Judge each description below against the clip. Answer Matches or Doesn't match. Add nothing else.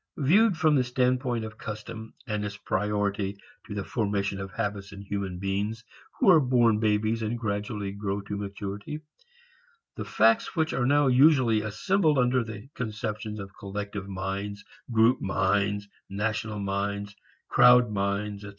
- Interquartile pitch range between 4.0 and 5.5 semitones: Doesn't match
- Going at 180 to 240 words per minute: Doesn't match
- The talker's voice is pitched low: Matches